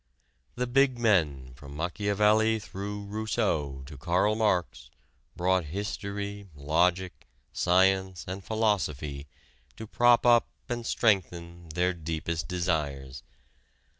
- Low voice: Yes, very low, 95 Hz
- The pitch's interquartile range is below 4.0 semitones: No, average, 4.6 semitones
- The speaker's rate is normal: No, slow, 105 wpm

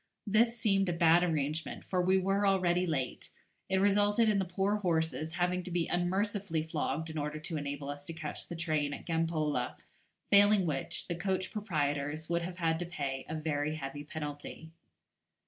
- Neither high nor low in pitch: Yes, medium, 165 Hz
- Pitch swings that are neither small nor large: Yes, average, 3.8 semitones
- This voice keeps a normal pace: Yes, average, 180 wpm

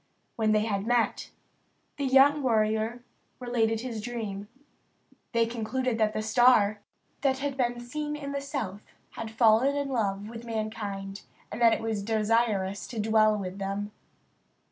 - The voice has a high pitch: Yes, high, 225 Hz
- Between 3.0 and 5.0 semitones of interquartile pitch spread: No, narrow, 2.5 semitones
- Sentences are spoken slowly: No, average, 150 wpm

